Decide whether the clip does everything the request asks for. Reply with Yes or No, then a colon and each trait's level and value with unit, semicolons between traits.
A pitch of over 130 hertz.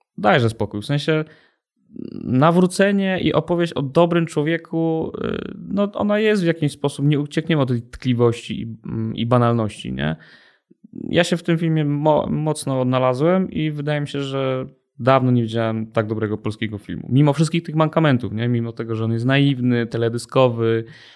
Yes: medium, 140 Hz